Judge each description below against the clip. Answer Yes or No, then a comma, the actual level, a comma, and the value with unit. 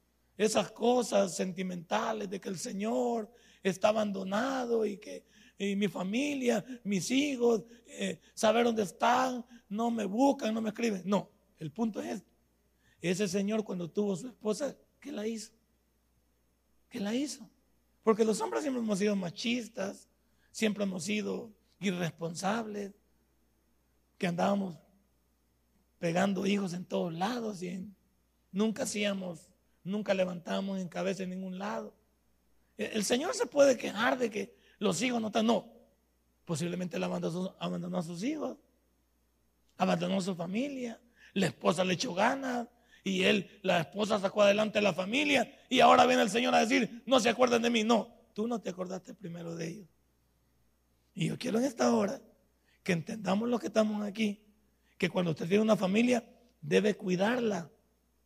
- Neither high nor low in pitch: No, high, 205 Hz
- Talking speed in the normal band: Yes, average, 150 wpm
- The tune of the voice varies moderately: Yes, average, 4.1 semitones